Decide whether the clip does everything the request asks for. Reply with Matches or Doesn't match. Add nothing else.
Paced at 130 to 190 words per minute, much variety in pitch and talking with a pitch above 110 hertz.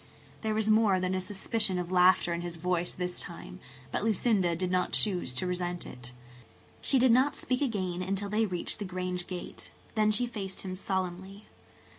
Doesn't match